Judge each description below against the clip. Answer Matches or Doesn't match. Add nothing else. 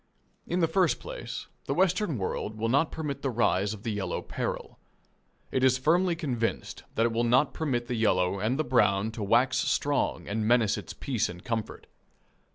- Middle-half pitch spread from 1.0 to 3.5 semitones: Doesn't match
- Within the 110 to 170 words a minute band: Doesn't match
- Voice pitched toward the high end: Doesn't match